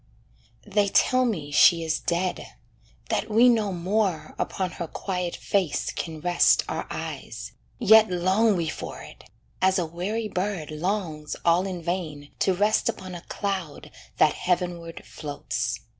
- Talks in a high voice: No, medium, 180 Hz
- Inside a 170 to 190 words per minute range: No, average, 145 wpm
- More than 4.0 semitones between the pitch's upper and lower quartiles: No, average, 3.3 semitones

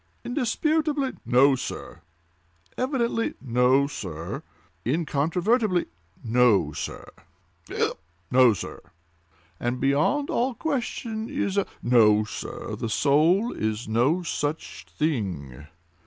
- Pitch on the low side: No, medium, 145 Hz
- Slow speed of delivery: Yes, slow, 95 wpm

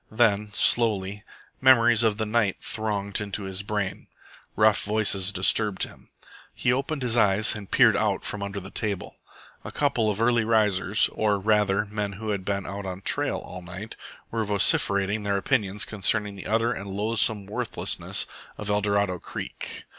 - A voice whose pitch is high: No, low, 105 Hz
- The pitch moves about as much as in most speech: No, narrow, 1.8 semitones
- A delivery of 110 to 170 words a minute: Yes, average, 160 wpm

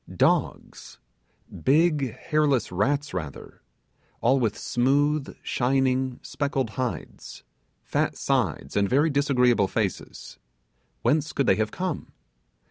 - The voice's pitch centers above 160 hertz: No, low, 135 Hz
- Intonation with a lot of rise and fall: No, average, 3.2 semitones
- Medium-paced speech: No, slow, 105 wpm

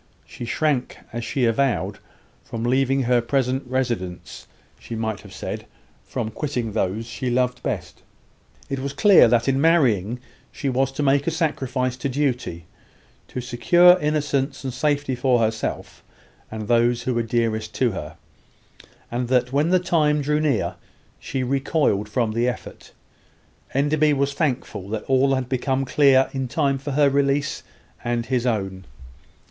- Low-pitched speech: Yes, low, 130 Hz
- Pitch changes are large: No, average, 3.0 semitones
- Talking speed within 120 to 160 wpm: Yes, average, 155 wpm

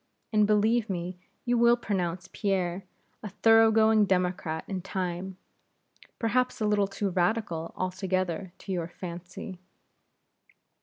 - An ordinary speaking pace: No, slow, 115 wpm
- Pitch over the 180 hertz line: Yes, high, 190 Hz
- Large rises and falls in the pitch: No, average, 3.1 semitones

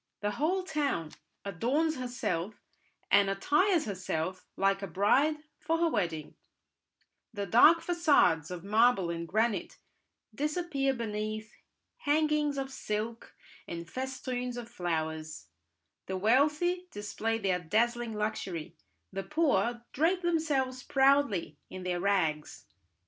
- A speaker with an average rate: No, slow, 115 wpm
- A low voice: No, high, 230 Hz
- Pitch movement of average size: No, wide, 7.3 semitones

